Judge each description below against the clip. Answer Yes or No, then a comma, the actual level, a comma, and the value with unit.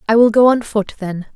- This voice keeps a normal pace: No, fast, 265 wpm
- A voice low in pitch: No, high, 220 Hz